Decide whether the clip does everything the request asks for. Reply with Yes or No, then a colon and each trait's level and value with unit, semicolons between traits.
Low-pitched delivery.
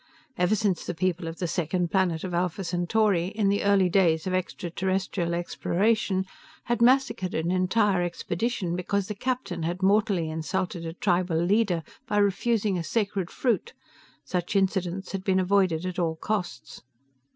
No: medium, 185 Hz